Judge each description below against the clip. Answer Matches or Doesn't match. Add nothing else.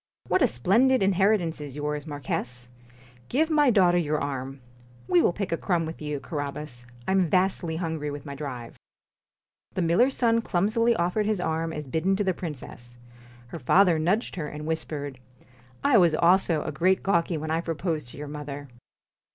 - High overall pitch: Doesn't match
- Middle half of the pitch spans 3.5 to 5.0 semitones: Matches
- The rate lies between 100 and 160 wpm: Doesn't match